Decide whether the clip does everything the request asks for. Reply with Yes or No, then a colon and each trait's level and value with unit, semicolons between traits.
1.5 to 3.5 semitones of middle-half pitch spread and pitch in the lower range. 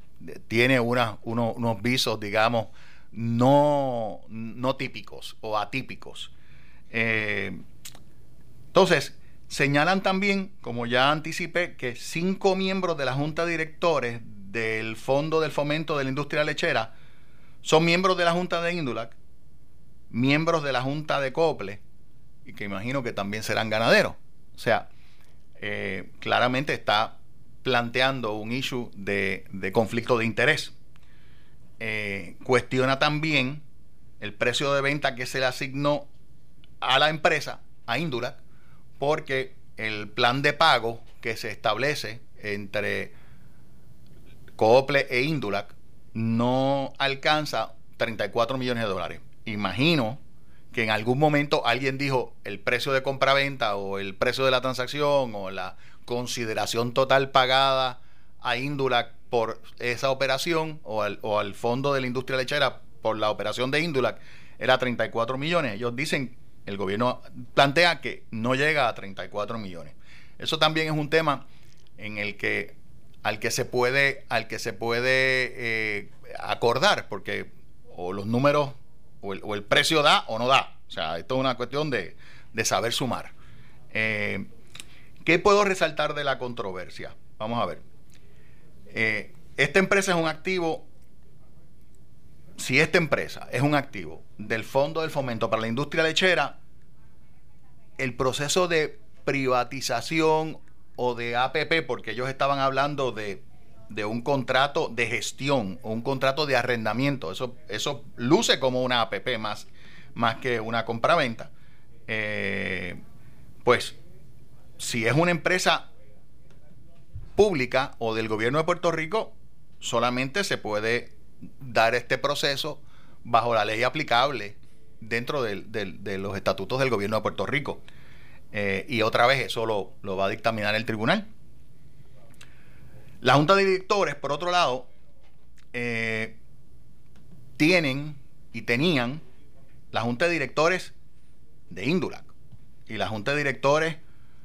No: average, 4.4 semitones; low, 130 Hz